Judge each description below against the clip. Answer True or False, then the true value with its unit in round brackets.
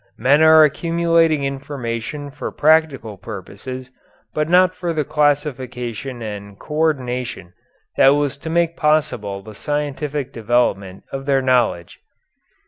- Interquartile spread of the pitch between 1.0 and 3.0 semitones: False (4.3 semitones)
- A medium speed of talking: False (125 wpm)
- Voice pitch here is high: False (140 Hz)